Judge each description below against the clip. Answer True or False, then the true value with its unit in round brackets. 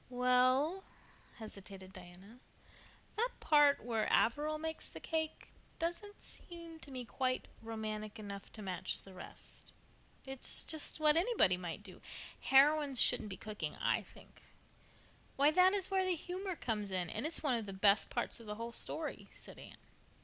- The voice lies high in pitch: True (255 Hz)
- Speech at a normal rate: True (160 wpm)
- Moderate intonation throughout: False (7.2 semitones)